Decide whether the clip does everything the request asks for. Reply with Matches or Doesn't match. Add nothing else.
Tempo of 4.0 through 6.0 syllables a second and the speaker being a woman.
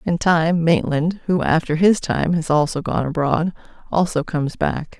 Matches